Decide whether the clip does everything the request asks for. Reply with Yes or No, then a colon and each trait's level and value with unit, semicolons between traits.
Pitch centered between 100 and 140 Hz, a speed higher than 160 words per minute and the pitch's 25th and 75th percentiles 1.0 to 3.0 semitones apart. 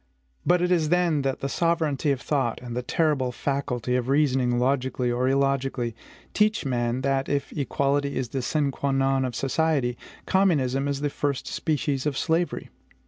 Yes: low, 135 Hz; average, 170 wpm; average, 2.7 semitones